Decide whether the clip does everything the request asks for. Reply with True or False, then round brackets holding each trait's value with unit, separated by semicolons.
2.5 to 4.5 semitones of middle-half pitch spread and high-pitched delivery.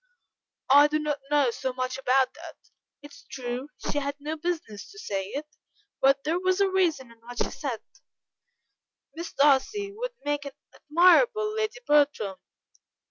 False (5.0 semitones; 290 Hz)